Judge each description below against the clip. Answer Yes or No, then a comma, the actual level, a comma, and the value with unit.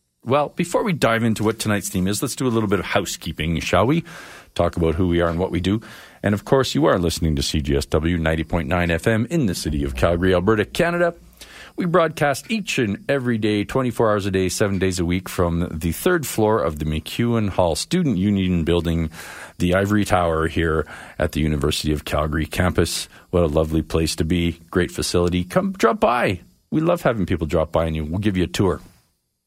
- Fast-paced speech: Yes, fast, 210 wpm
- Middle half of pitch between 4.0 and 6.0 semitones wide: Yes, average, 5.2 semitones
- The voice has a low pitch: Yes, very low, 90 Hz